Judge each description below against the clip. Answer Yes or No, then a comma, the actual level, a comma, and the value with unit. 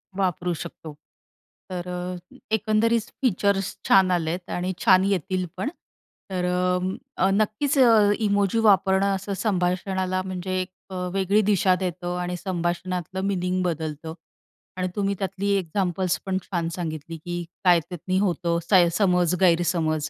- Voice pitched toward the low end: No, medium, 185 Hz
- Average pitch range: No, narrow, 1.9 semitones